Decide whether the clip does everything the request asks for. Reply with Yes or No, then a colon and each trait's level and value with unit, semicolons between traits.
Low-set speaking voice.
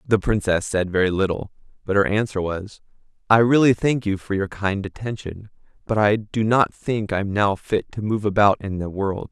Yes: low, 100 Hz